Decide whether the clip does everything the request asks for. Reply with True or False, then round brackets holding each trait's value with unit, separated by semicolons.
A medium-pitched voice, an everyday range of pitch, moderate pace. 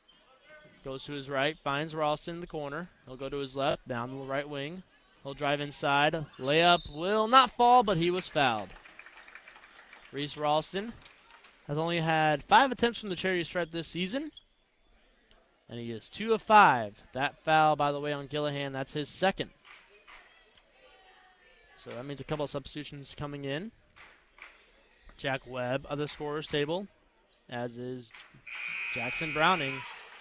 True (150 Hz; 3.9 semitones; 155 wpm)